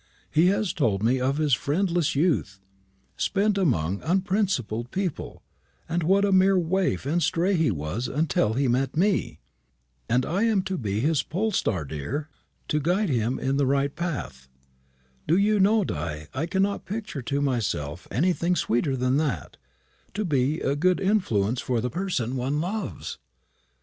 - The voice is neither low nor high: Yes, medium, 150 Hz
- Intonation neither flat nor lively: No, wide, 7.1 semitones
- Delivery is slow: No, average, 160 wpm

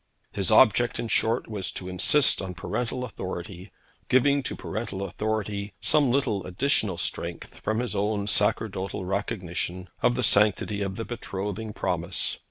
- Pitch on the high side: No, low, 105 Hz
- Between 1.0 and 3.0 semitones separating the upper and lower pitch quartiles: No, average, 3.5 semitones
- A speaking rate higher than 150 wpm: No, average, 145 wpm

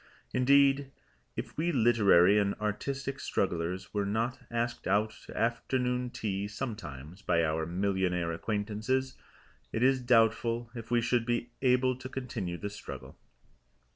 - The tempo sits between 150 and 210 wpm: No, slow, 135 wpm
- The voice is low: Yes, low, 115 Hz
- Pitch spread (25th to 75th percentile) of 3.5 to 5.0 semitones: Yes, average, 4.1 semitones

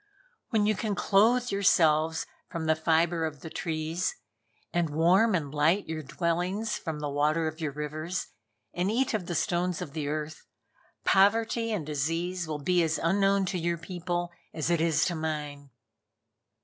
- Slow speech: No, average, 165 wpm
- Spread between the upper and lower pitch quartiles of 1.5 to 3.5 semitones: Yes, average, 2.9 semitones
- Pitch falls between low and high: Yes, medium, 170 Hz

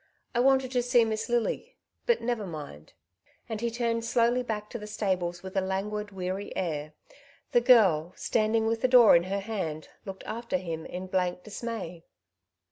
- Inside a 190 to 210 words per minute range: No, average, 175 wpm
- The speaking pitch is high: Yes, high, 210 Hz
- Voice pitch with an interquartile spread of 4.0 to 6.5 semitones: Yes, average, 4.3 semitones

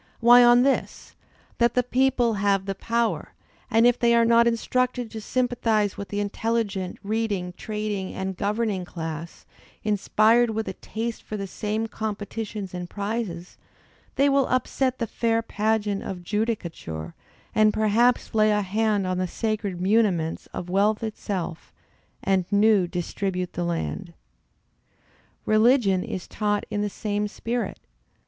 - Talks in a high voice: Yes, high, 215 Hz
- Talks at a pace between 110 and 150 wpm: Yes, average, 140 wpm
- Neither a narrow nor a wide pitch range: Yes, average, 3.1 semitones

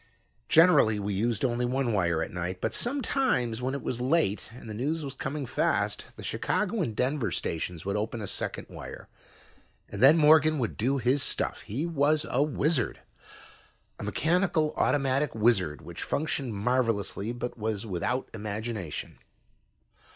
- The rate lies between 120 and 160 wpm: Yes, average, 155 wpm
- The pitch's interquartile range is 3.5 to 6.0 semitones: Yes, wide, 5.6 semitones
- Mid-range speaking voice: No, low, 125 Hz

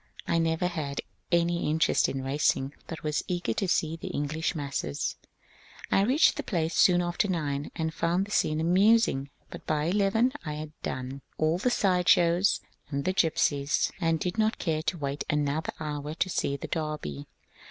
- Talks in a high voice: No, medium, 160 Hz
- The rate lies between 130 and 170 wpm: No, average, 185 wpm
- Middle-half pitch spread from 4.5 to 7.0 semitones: No, average, 3.3 semitones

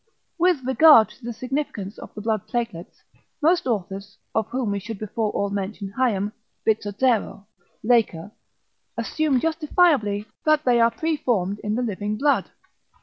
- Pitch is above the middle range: Yes, high, 225 Hz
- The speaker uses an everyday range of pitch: Yes, average, 4.5 semitones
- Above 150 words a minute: No, average, 145 wpm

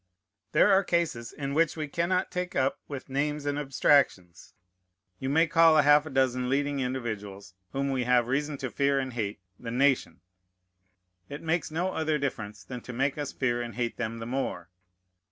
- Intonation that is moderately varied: Yes, average, 3.6 semitones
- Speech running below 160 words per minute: No, average, 180 wpm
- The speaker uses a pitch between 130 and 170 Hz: Yes, low, 135 Hz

